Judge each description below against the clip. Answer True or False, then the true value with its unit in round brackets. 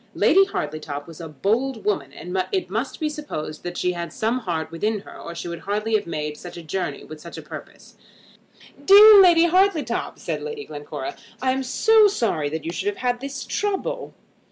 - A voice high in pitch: True (210 Hz)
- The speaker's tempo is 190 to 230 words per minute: True (200 wpm)